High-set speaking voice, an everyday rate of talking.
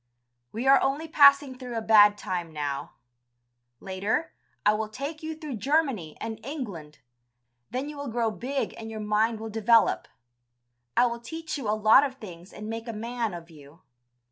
Yes: high, 225 Hz; average, 175 wpm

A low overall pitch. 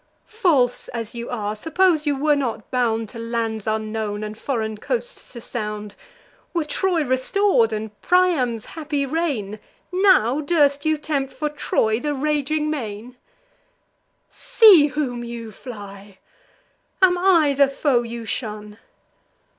No: very high, 260 Hz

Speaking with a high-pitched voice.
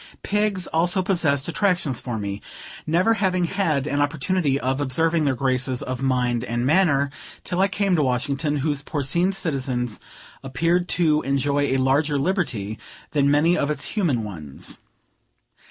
No: medium, 145 Hz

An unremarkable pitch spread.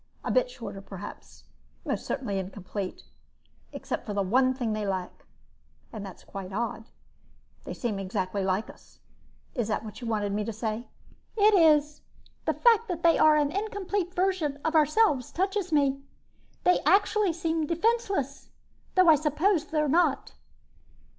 No: wide, 8.9 semitones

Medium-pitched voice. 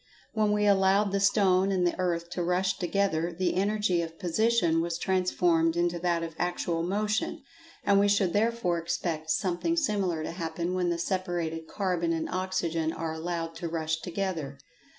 Yes: medium, 175 Hz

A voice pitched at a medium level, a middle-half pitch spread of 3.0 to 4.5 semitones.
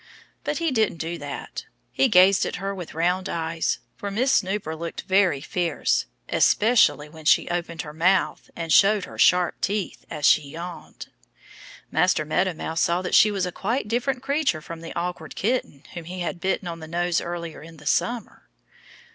Yes: medium, 175 Hz; average, 3.3 semitones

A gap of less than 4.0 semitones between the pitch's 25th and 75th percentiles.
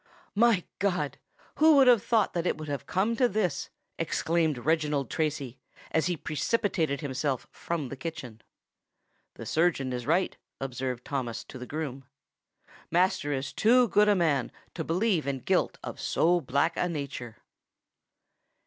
No: average, 5.1 semitones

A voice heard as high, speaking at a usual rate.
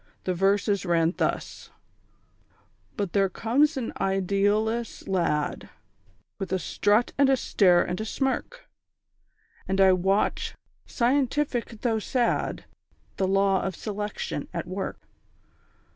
No: high, 200 Hz; slow, 115 wpm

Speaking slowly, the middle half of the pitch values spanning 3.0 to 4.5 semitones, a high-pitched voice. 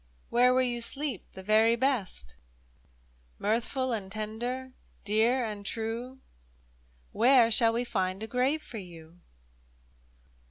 Yes: slow, 125 wpm; average, 4.1 semitones; high, 225 Hz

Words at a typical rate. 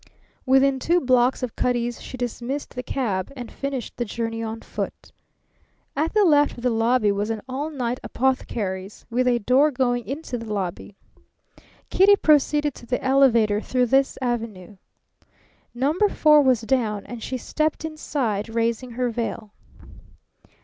Yes: average, 150 wpm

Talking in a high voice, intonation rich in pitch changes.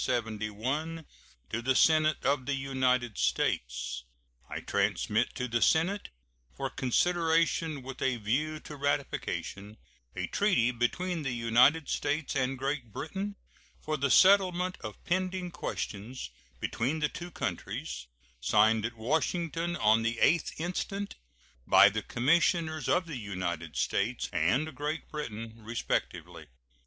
No: low, 135 Hz; wide, 6.2 semitones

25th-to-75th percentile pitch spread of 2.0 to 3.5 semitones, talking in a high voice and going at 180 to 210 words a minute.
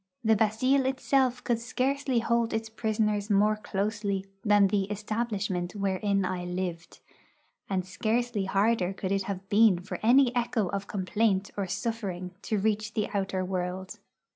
No: average, 2.8 semitones; high, 205 Hz; average, 145 wpm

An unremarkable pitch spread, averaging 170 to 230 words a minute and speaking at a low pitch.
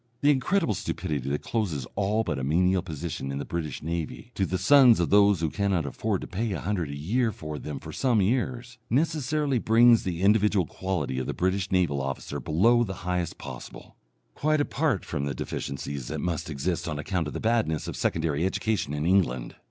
No: wide, 6.6 semitones; average, 200 wpm; very low, 90 Hz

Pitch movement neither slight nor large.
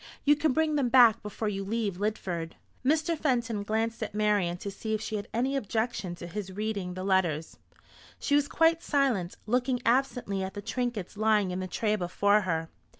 Yes: average, 4.5 semitones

